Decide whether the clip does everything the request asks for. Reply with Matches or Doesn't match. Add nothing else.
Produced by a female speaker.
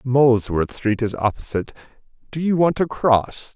Doesn't match